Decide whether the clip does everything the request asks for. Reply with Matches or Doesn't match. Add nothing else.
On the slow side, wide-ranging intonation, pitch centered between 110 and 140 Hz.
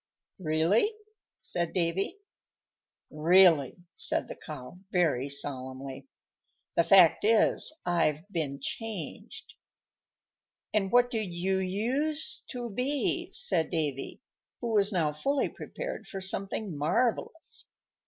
Doesn't match